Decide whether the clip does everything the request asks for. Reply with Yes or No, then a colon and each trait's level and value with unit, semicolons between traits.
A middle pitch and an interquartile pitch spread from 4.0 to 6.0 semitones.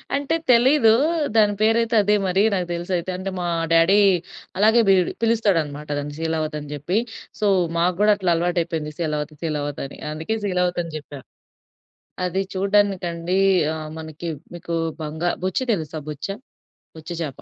Yes: medium, 175 Hz; average, 4.4 semitones